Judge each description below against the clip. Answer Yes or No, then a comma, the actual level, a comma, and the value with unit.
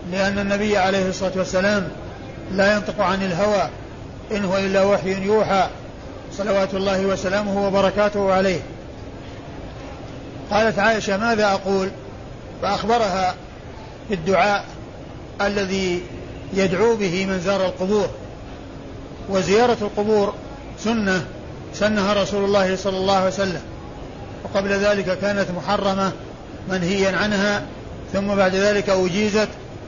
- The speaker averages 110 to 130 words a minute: No, average, 100 wpm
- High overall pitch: Yes, high, 195 Hz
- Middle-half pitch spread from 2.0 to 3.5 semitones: No, narrow, 1.5 semitones